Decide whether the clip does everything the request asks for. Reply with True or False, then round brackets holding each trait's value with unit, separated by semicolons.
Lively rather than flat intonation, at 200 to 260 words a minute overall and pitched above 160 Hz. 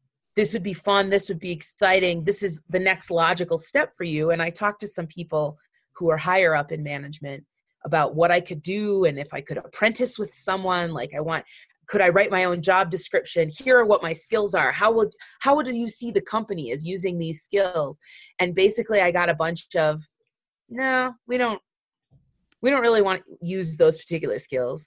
False (3.9 semitones; 205 wpm; 185 Hz)